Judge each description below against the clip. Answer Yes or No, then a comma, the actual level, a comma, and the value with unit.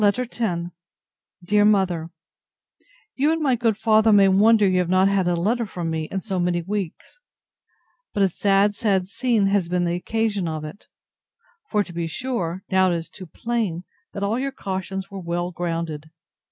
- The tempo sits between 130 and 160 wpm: No, average, 180 wpm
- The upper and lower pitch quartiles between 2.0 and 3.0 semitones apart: No, average, 3.4 semitones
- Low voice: No, high, 195 Hz